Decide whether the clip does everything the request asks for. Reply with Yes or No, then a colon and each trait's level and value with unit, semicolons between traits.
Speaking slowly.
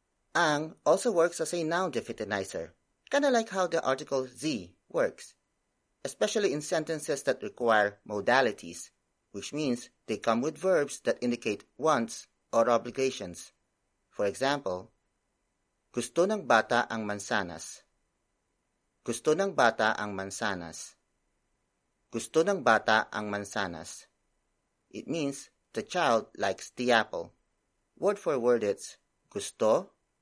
Yes: slow, 120 wpm